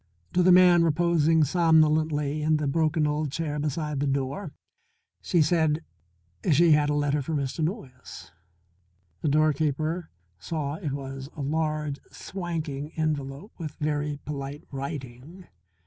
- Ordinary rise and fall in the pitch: No, narrow, 2.3 semitones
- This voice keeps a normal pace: No, slow, 130 wpm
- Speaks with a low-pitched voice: No, medium, 150 Hz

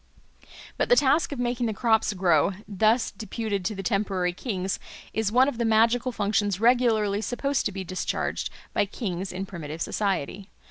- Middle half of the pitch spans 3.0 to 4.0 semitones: Yes, average, 3.6 semitones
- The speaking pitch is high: Yes, high, 210 Hz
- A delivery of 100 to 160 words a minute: No, average, 170 wpm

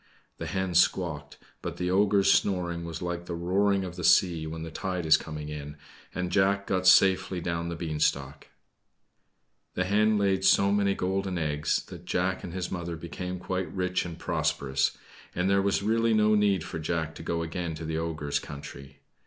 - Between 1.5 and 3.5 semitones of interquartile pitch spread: Yes, average, 2.9 semitones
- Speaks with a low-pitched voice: Yes, very low, 90 Hz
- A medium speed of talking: Yes, average, 185 wpm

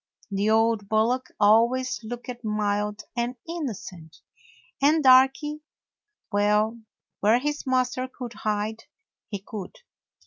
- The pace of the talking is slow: Yes, slow, 110 wpm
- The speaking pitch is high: Yes, high, 230 Hz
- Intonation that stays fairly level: No, average, 3.6 semitones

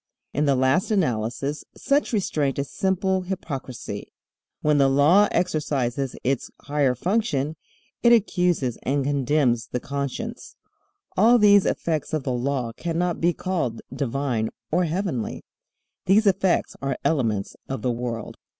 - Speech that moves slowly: Yes, slow, 130 wpm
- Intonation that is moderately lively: No, wide, 5.9 semitones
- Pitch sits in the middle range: Yes, medium, 145 Hz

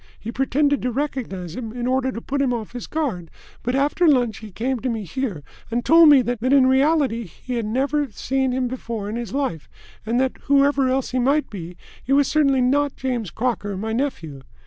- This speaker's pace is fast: Yes, fast, 210 wpm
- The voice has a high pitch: Yes, very high, 255 Hz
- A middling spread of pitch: Yes, average, 3.5 semitones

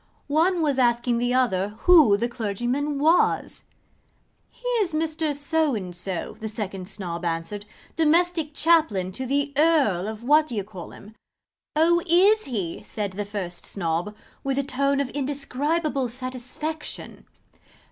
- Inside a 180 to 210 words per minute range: No, slow, 135 wpm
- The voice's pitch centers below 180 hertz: No, very high, 255 Hz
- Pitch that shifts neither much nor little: No, wide, 6.9 semitones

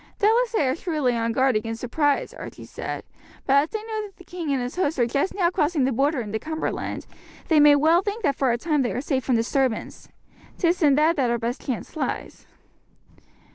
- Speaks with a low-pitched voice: No, very high, 285 Hz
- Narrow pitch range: No, average, 5.2 semitones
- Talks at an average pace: No, fast, 215 wpm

